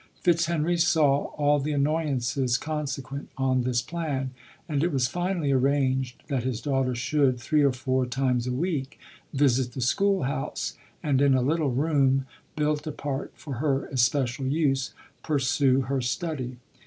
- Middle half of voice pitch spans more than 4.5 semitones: No, average, 2.7 semitones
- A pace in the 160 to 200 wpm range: No, average, 150 wpm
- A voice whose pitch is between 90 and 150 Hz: Yes, low, 135 Hz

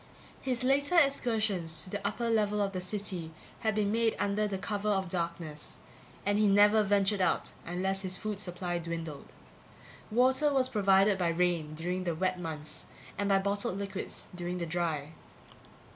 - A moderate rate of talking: Yes, average, 160 wpm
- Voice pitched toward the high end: Yes, high, 195 Hz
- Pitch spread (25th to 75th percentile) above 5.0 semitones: No, average, 3.3 semitones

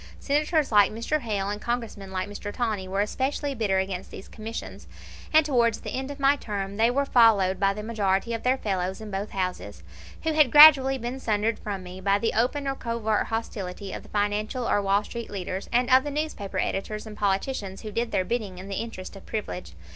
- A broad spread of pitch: No, average, 3.9 semitones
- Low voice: No, high, 215 Hz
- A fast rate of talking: Yes, fast, 210 wpm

